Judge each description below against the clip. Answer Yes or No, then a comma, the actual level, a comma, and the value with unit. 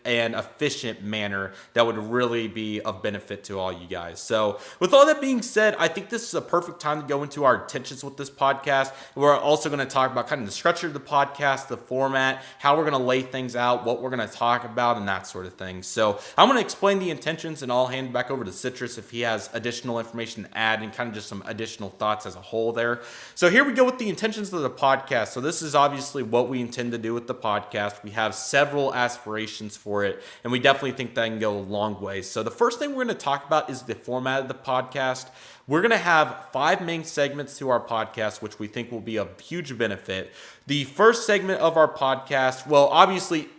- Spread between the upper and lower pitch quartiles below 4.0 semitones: No, average, 4.5 semitones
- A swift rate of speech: Yes, fast, 245 wpm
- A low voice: Yes, low, 130 Hz